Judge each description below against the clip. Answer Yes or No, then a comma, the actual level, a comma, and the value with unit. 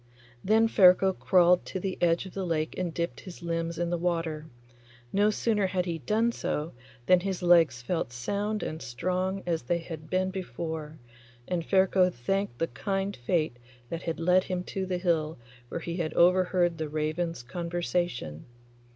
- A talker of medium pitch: Yes, medium, 175 Hz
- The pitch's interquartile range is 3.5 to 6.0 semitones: No, narrow, 2.6 semitones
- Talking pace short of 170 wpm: No, average, 175 wpm